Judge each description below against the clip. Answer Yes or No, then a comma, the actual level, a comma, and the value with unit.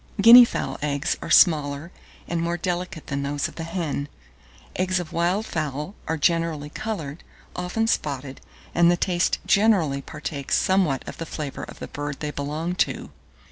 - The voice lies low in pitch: No, medium, 165 Hz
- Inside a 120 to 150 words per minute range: No, average, 165 wpm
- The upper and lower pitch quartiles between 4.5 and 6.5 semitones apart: No, average, 3.7 semitones